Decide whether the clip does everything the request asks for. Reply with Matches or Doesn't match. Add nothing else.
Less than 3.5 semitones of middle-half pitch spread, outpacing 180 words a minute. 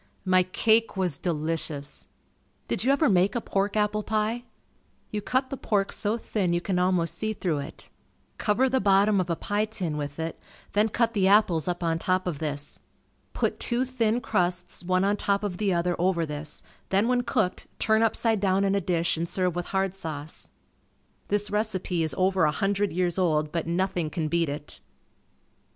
Doesn't match